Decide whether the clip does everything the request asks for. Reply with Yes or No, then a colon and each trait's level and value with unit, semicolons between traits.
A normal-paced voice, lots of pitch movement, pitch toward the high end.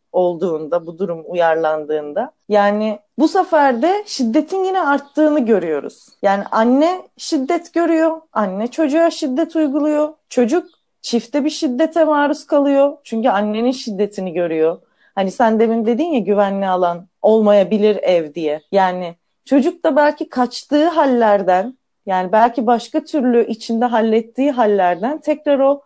Yes: average, 130 wpm; wide, 7.0 semitones; high, 245 Hz